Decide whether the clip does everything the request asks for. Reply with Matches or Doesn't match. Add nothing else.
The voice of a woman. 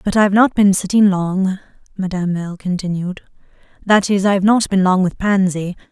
Matches